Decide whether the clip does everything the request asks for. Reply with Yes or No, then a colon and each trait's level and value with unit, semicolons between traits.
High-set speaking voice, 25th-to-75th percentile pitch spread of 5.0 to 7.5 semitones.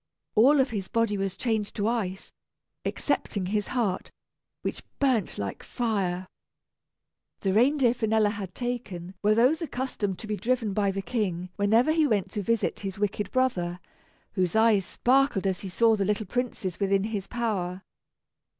No: high, 210 Hz; average, 3.6 semitones